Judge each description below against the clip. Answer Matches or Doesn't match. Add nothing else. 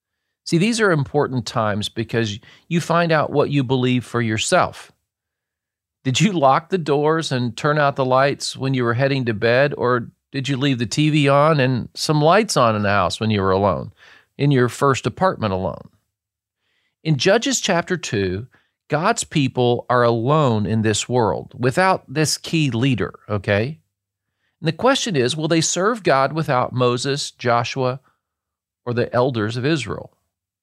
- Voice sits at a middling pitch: Doesn't match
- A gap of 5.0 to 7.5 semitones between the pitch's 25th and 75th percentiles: Matches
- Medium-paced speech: Matches